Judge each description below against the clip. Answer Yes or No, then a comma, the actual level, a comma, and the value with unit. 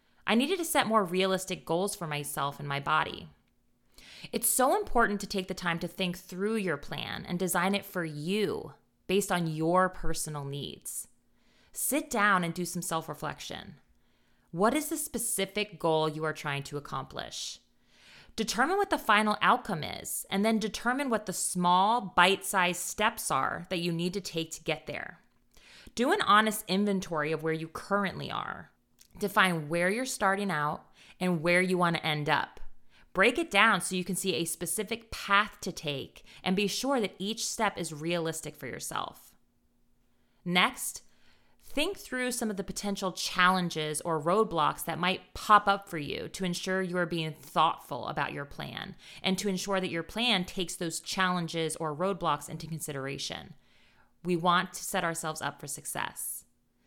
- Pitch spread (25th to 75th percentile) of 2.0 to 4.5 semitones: Yes, average, 3.8 semitones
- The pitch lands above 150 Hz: Yes, medium, 185 Hz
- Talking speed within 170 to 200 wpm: Yes, average, 175 wpm